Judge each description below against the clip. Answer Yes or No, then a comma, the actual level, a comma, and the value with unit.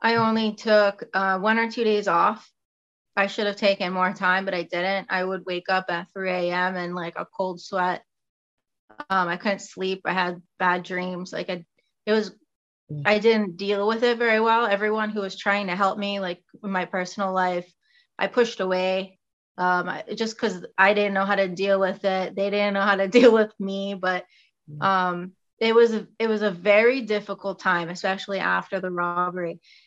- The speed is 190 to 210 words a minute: Yes, average, 195 wpm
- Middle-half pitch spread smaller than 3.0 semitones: Yes, narrow, 2.4 semitones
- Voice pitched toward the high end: Yes, high, 195 Hz